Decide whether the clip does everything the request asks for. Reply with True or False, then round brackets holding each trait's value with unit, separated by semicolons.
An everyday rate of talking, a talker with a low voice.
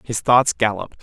True (175 wpm; 115 Hz)